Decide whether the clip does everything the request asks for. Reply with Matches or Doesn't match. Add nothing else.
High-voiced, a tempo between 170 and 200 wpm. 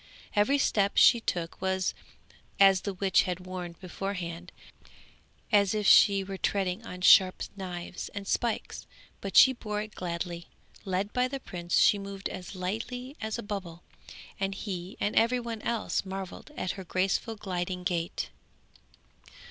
Doesn't match